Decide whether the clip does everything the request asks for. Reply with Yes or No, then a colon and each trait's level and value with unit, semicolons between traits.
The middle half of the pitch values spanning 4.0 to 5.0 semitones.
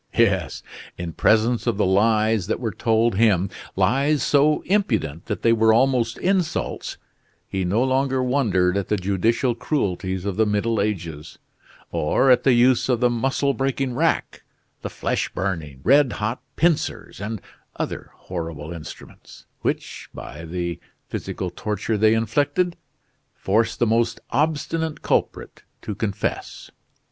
No: wide, 5.4 semitones